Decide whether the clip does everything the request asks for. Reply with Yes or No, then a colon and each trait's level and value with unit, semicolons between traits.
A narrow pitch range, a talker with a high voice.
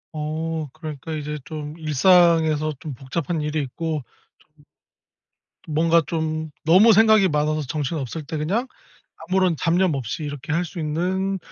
No: narrow, 2.2 semitones; medium, 155 Hz